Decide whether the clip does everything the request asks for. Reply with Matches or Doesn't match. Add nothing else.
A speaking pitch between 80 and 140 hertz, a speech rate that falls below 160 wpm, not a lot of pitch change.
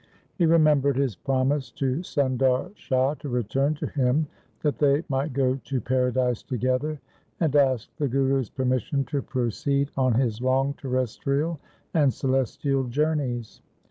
Matches